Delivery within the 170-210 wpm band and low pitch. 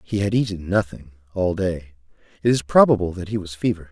Yes: average, 200 wpm; very low, 95 Hz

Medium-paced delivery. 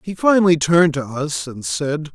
Yes: average, 195 wpm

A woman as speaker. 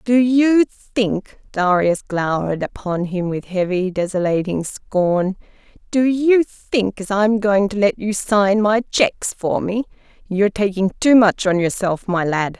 Yes: female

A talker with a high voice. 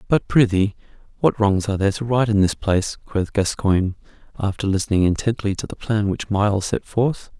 No: low, 105 Hz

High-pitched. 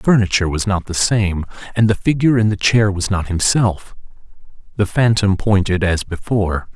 No: low, 100 Hz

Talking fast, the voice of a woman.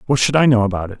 No: fast, 360 wpm; male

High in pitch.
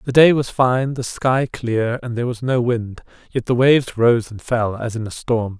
No: low, 120 Hz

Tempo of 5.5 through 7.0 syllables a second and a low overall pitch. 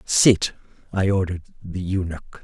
No: 4.5 syllables/s; very low, 90 Hz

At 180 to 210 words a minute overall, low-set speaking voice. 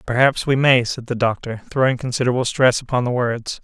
Yes: average, 200 wpm; low, 125 Hz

